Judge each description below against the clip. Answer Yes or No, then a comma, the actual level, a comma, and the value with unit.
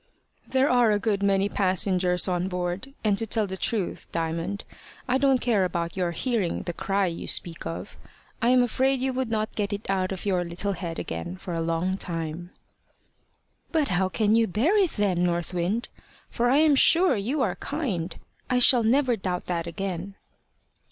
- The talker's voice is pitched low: No, high, 195 Hz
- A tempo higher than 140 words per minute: Yes, average, 185 wpm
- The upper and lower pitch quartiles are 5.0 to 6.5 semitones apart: Yes, wide, 5.4 semitones